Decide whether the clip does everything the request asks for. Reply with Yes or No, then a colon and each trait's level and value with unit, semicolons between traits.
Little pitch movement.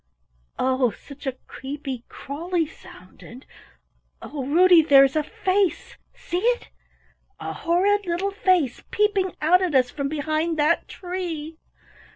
No: average, 4.7 semitones